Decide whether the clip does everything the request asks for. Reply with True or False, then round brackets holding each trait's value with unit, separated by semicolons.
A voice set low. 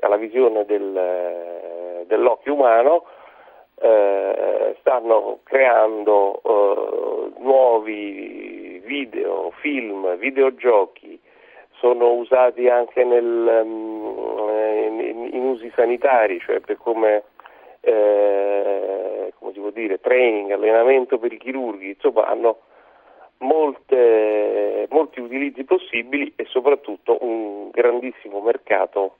True (120 Hz)